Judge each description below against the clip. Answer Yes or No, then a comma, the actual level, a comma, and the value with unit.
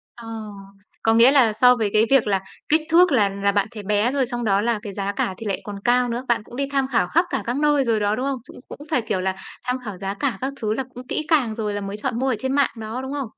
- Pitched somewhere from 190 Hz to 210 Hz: No, high, 235 Hz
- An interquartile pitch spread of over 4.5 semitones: No, average, 4.0 semitones